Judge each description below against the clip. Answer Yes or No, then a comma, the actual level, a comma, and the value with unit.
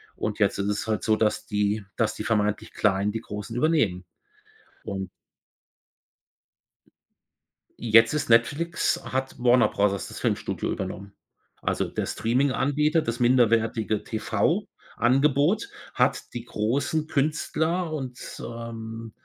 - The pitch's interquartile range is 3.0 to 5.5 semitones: Yes, average, 4.7 semitones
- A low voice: Yes, low, 115 Hz